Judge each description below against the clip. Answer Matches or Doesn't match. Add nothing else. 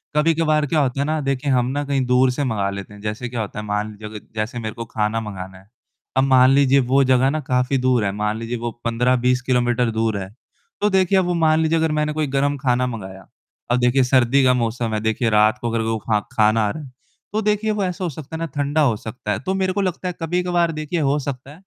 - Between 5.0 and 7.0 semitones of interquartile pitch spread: Matches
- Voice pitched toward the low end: Matches